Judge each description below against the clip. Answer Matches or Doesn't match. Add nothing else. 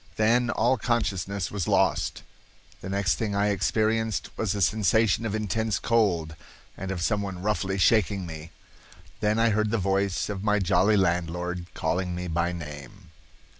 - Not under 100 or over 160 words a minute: Matches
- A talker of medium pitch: Doesn't match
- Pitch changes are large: Doesn't match